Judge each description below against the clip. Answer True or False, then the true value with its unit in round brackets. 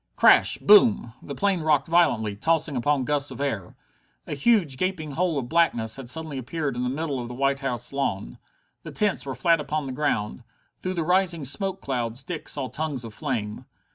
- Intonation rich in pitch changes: False (4.8 semitones)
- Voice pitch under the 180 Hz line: True (140 Hz)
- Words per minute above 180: True (195 wpm)